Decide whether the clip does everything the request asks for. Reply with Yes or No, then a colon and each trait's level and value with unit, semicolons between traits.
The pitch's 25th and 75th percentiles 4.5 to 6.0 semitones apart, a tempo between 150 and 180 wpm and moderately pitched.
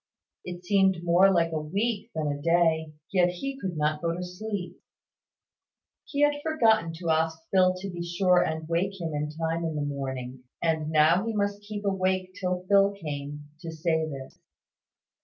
No: average, 3.5 semitones; average, 175 wpm; medium, 175 Hz